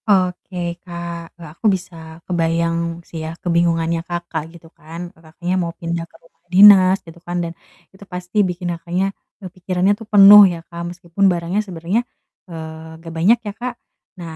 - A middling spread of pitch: No, narrow, 1.8 semitones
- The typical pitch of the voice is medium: Yes, medium, 175 Hz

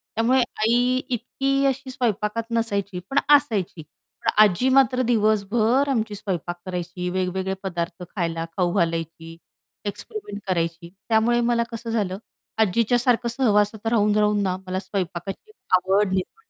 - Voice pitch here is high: Yes, high, 210 Hz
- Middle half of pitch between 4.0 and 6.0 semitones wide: Yes, average, 4.6 semitones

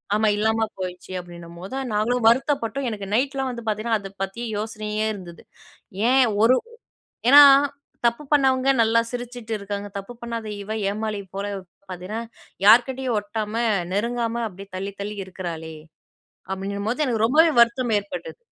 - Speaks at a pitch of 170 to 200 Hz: No, high, 220 Hz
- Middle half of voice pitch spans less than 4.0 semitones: Yes, average, 3.3 semitones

